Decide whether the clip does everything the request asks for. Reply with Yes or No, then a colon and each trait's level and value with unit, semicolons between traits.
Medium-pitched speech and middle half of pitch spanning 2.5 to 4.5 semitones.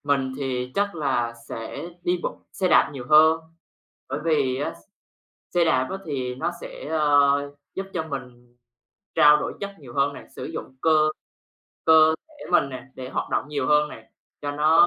Yes: medium, 145 Hz; average, 3.5 semitones